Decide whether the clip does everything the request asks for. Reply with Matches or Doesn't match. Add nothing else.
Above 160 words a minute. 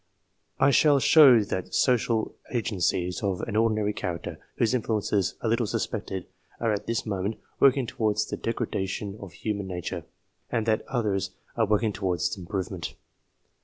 Doesn't match